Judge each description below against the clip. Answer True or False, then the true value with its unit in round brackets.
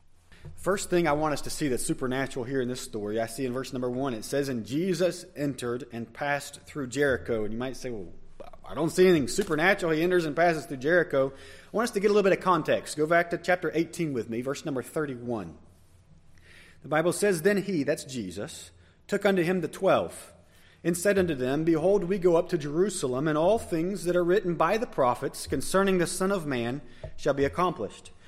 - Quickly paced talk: True (220 wpm)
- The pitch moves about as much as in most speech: False (6.6 semitones)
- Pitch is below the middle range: False (150 Hz)